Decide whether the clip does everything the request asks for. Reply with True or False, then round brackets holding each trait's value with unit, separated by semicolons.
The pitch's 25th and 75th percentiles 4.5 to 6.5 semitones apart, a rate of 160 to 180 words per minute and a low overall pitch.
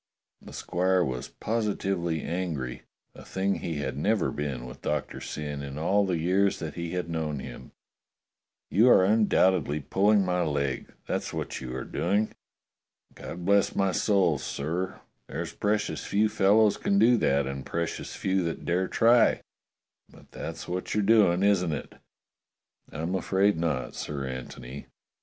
False (5.2 semitones; 150 wpm; 90 Hz)